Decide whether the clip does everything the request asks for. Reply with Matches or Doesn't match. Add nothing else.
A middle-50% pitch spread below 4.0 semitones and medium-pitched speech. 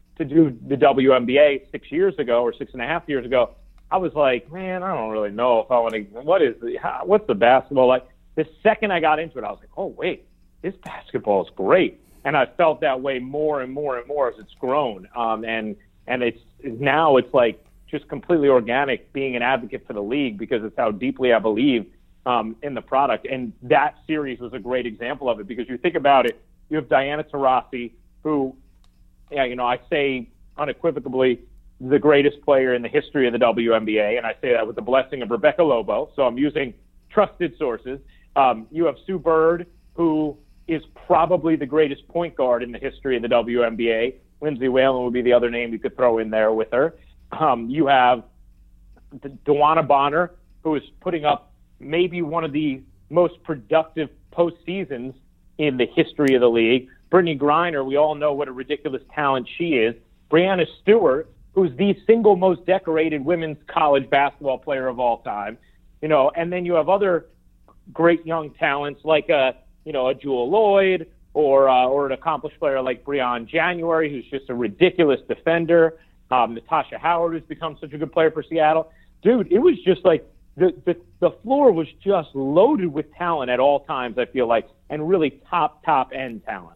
Doesn't match